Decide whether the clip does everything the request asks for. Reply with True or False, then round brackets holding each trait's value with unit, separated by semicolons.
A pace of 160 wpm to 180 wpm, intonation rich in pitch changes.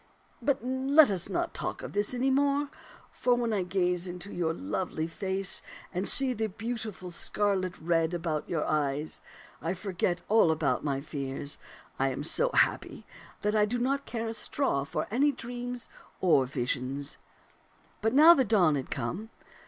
True (170 wpm; 7.1 semitones)